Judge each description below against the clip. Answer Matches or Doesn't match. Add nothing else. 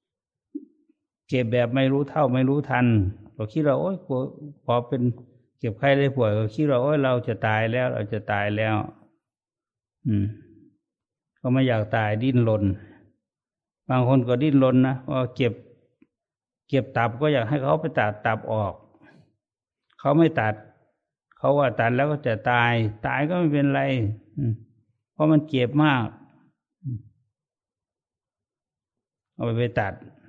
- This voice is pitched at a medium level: Doesn't match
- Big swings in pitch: Doesn't match